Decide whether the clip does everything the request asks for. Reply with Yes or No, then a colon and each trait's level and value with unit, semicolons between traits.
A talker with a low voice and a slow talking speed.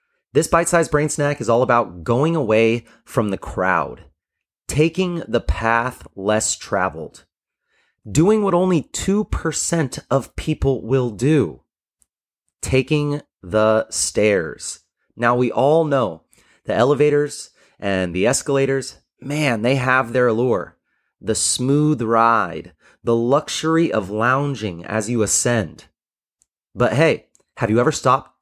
Yes: low, 130 Hz; slow, 120 wpm